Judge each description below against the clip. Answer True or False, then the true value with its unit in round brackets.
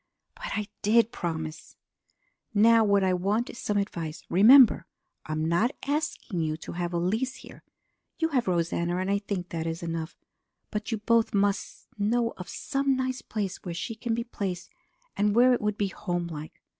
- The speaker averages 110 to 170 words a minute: False (180 wpm)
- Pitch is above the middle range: True (200 Hz)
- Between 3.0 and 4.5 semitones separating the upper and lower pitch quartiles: False (5.1 semitones)